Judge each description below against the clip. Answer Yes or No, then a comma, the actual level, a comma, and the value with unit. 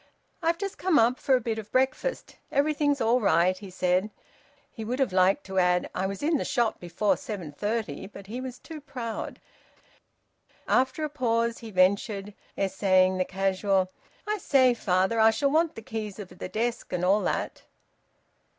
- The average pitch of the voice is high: Yes, high, 220 Hz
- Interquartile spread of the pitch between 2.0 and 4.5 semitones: No, average, 5.3 semitones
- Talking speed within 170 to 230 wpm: Yes, average, 180 wpm